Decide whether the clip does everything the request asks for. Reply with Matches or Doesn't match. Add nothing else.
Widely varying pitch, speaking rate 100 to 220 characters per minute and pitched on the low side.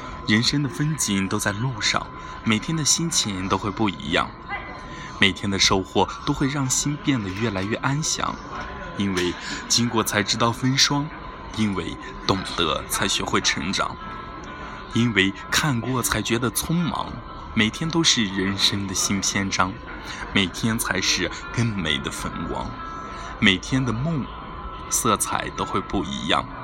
Matches